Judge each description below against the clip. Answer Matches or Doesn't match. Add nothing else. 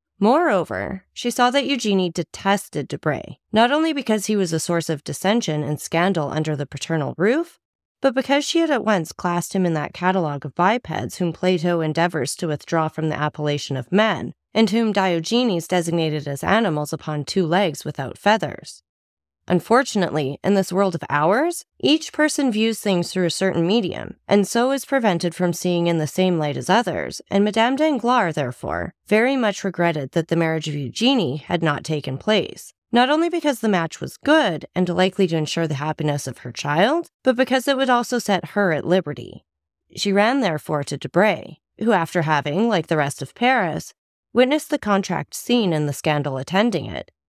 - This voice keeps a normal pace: Matches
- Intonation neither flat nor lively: Doesn't match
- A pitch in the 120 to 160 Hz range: Doesn't match